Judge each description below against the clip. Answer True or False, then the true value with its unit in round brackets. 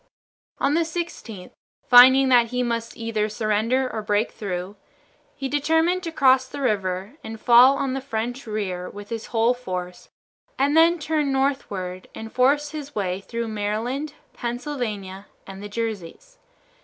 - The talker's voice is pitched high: True (235 Hz)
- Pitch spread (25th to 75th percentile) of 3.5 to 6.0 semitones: True (4.8 semitones)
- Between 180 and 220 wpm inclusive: False (150 wpm)